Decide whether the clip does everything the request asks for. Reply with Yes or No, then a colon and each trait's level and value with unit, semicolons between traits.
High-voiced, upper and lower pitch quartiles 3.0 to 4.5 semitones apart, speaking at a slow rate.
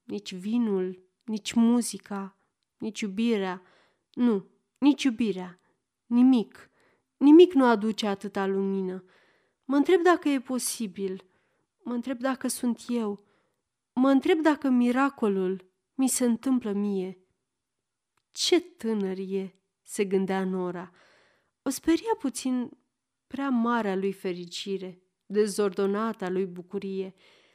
No: high, 215 Hz; average, 5.2 semitones; slow, 105 wpm